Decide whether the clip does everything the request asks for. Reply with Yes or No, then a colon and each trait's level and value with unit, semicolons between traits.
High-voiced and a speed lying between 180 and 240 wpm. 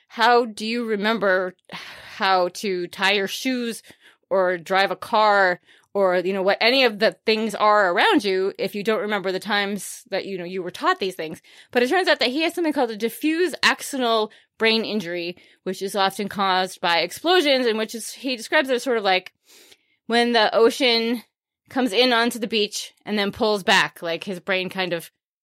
Yes: high, 215 Hz; average, 200 wpm